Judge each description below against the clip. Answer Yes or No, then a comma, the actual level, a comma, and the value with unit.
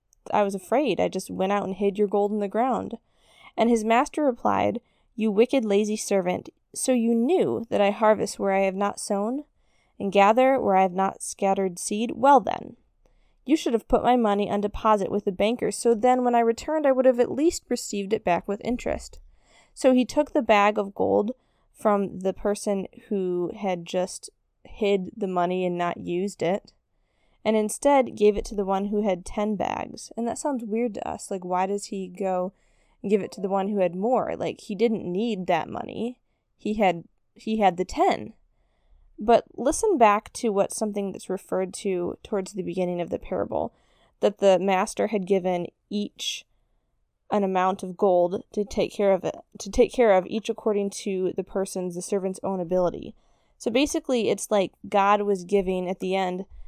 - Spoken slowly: No, average, 195 wpm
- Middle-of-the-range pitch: No, high, 205 Hz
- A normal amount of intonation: Yes, average, 3.2 semitones